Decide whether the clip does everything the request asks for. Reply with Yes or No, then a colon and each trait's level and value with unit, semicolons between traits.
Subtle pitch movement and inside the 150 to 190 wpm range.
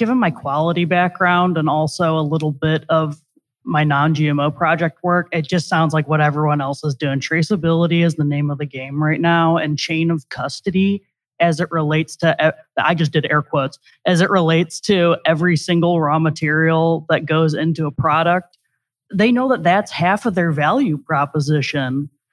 Yes: narrow, 2.3 semitones; average, 185 wpm